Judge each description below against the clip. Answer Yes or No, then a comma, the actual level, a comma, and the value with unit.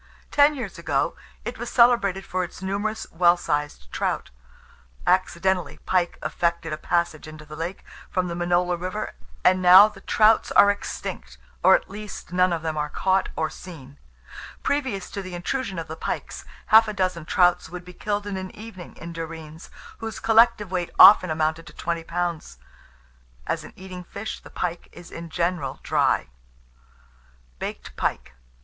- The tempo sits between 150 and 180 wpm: Yes, average, 165 wpm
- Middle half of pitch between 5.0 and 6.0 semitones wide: No, average, 3.1 semitones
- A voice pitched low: No, medium, 180 Hz